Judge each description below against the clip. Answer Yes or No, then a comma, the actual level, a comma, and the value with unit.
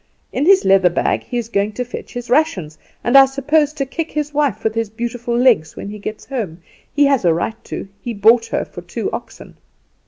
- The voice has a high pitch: Yes, high, 240 Hz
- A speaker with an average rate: No, fast, 220 wpm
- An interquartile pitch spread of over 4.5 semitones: Yes, average, 5.0 semitones